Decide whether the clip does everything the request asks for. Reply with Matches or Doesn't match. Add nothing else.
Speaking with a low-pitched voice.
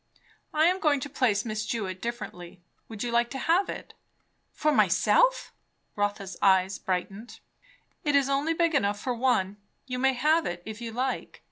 Doesn't match